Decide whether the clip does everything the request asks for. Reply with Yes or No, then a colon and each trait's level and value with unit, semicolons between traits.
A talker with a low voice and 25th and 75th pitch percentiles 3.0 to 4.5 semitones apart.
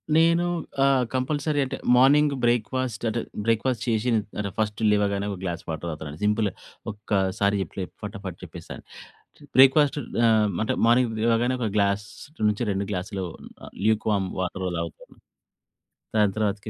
Yes: low, 105 Hz; average, 4.0 semitones